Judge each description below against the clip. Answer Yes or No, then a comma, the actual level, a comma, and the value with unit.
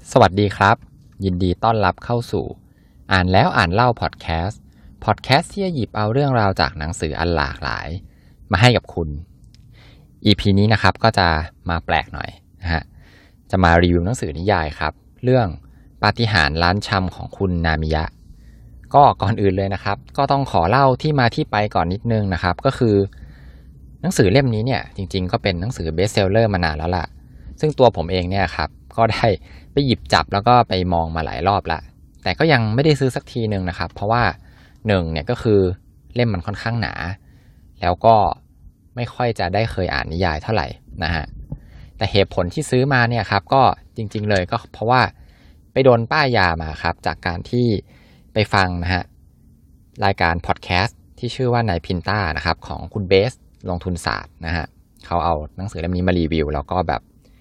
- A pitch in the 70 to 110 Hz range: Yes, very low, 95 Hz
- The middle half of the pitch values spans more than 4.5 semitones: Yes, wide, 5.4 semitones